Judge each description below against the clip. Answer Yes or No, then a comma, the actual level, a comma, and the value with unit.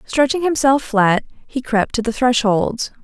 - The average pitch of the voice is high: Yes, high, 245 Hz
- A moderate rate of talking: Yes, average, 160 wpm